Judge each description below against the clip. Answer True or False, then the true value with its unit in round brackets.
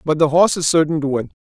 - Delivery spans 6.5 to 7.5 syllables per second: True (7.3 syllables/s)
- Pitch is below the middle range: False (155 Hz)